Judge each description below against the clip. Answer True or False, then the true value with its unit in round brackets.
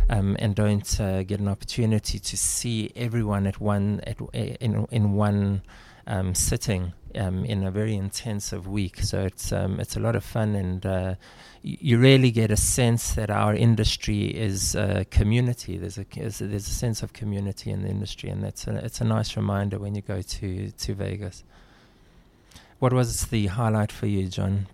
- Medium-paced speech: True (190 wpm)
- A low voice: True (105 Hz)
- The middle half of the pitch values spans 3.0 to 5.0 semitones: False (2.4 semitones)